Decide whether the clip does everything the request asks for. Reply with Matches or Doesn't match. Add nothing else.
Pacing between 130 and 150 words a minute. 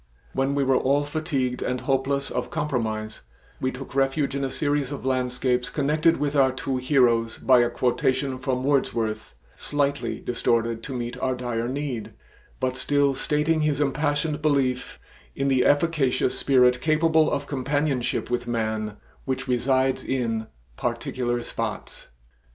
Matches